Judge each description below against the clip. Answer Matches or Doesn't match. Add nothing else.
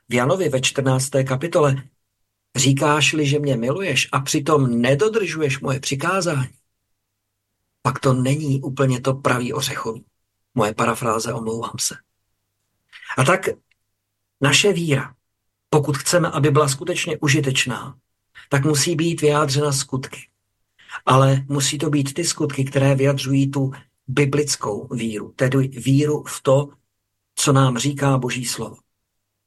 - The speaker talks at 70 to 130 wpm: Matches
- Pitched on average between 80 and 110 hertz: Doesn't match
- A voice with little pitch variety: Doesn't match